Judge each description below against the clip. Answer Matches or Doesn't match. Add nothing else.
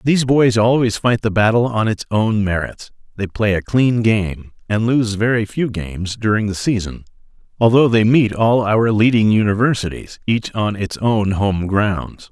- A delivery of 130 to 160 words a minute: Doesn't match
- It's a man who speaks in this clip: Matches